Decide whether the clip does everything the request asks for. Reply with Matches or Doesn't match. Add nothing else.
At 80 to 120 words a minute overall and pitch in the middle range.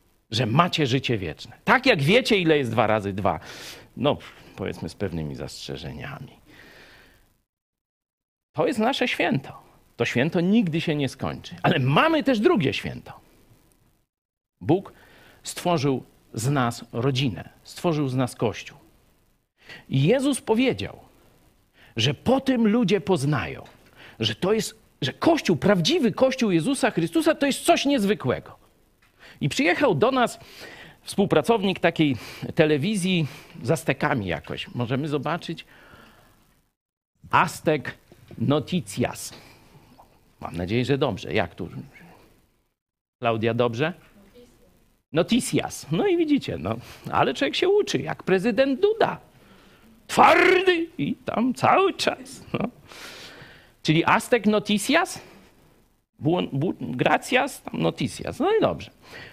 Matches